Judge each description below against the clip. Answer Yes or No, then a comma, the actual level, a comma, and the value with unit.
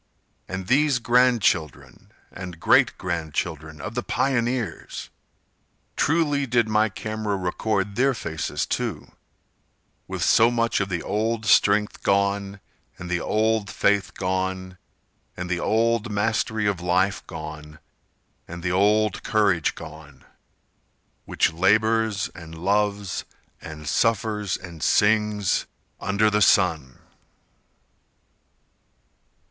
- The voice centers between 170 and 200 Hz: No, low, 100 Hz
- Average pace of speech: No, slow, 110 wpm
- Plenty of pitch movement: No, average, 3.7 semitones